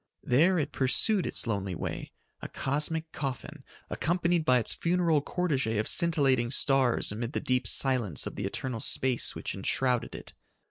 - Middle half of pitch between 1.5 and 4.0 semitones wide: No, average, 5.2 semitones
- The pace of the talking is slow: No, average, 155 wpm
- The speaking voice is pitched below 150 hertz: Yes, low, 135 Hz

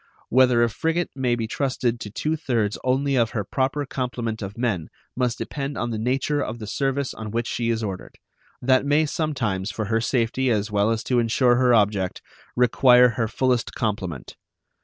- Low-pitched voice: Yes, low, 120 Hz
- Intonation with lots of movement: No, average, 3.1 semitones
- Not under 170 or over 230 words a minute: Yes, average, 185 wpm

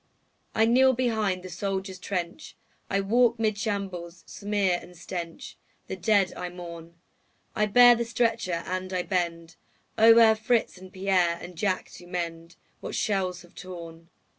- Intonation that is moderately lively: Yes, average, 3.7 semitones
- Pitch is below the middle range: No, medium, 185 Hz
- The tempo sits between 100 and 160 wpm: Yes, average, 150 wpm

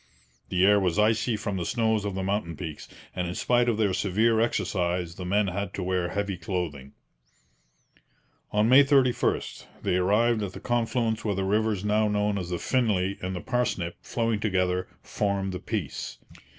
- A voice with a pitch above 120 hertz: No, low, 100 Hz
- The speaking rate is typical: Yes, average, 175 wpm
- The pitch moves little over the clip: No, average, 3.3 semitones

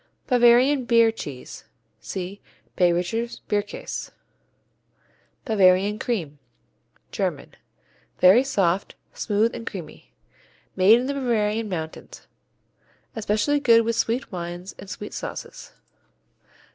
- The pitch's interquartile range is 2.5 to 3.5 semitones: No, average, 4.3 semitones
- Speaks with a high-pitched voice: Yes, high, 210 Hz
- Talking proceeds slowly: Yes, slow, 95 wpm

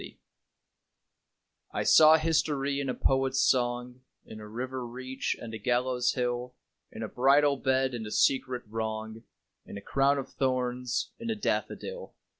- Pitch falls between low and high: No, low, 130 Hz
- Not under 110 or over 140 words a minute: No, average, 155 wpm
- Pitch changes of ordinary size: No, narrow, 2.0 semitones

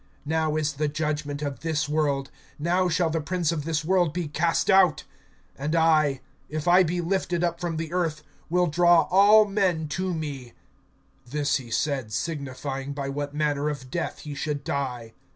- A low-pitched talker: No, medium, 155 Hz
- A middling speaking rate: Yes, average, 175 wpm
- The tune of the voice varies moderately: Yes, average, 3.1 semitones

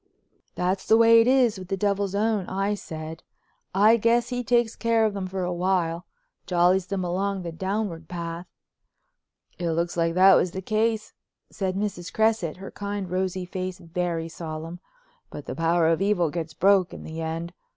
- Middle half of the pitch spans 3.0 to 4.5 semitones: Yes, average, 3.3 semitones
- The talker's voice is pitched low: No, medium, 185 Hz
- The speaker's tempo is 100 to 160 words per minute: No, average, 180 wpm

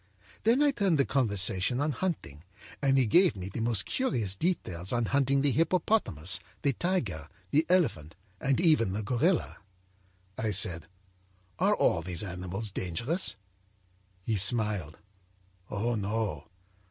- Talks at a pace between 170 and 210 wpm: No, slow, 135 wpm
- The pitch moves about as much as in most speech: No, wide, 8.3 semitones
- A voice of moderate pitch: No, low, 115 Hz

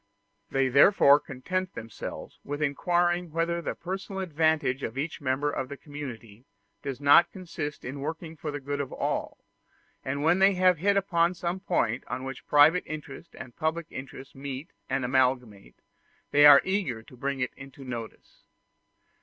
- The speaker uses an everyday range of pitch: Yes, average, 4.3 semitones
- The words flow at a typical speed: Yes, average, 160 wpm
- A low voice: No, medium, 145 Hz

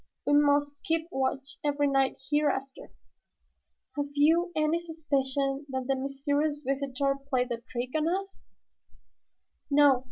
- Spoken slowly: Yes, slow, 120 wpm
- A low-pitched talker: No, very high, 285 Hz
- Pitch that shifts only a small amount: Yes, narrow, 2.0 semitones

